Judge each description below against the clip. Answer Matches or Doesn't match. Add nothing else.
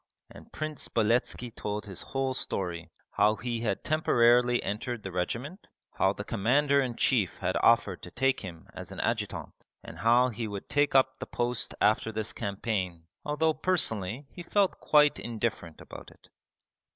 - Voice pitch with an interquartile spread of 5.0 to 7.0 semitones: Doesn't match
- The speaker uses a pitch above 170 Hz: Doesn't match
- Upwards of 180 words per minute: Doesn't match